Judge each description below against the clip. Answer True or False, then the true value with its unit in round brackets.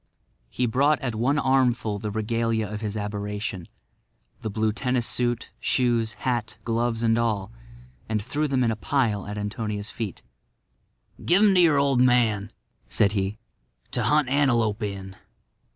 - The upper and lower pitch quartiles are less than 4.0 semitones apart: True (3.3 semitones)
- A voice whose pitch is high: False (115 Hz)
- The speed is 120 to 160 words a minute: True (150 wpm)